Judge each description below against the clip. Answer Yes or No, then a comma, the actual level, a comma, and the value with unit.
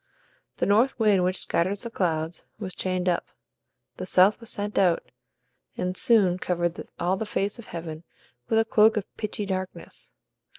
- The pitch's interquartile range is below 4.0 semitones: Yes, average, 2.9 semitones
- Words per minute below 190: Yes, average, 165 wpm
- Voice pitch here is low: No, high, 190 Hz